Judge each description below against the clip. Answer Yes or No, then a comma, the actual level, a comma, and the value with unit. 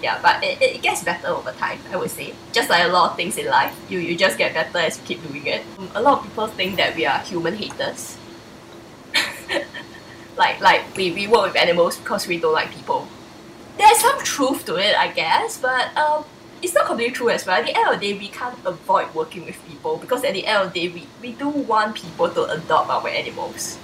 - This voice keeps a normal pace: No, fast, 235 wpm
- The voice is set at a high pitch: Yes, very high, 270 Hz